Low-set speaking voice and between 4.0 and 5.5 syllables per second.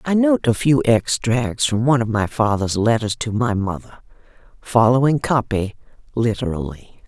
Yes: low, 120 Hz; 4.7 syllables/s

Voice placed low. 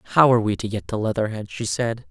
Yes: low, 115 Hz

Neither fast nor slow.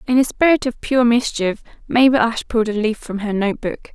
No: fast, 230 wpm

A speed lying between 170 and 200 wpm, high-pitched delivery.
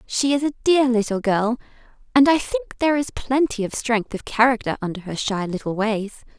Yes: average, 195 wpm; high, 230 Hz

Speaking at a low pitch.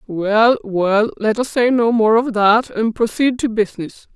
No: high, 220 Hz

